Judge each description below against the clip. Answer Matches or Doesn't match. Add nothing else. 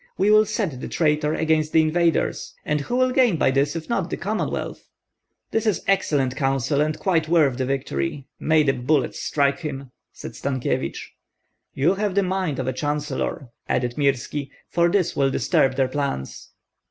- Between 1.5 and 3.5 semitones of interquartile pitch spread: Doesn't match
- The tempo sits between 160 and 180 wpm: Matches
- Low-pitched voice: Doesn't match